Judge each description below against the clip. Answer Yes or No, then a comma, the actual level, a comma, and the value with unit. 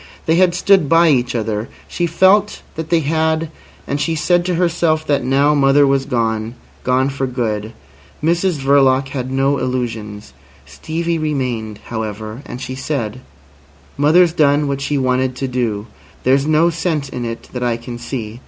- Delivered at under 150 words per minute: No, average, 160 wpm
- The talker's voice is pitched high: No, low, 135 Hz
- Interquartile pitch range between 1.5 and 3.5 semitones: No, average, 4.6 semitones